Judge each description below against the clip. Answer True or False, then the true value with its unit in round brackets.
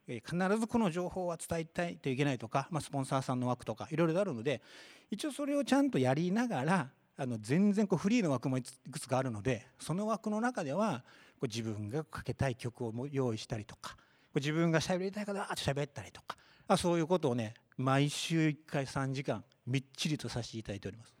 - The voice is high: False (140 Hz)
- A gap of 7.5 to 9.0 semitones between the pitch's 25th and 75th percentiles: False (6.0 semitones)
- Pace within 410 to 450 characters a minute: True (415 characters per minute)